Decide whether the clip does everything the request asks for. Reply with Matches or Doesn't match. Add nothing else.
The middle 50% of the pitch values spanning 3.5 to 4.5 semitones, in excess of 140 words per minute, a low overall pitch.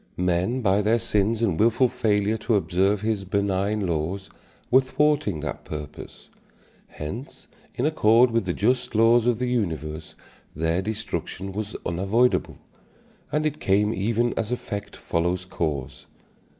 Doesn't match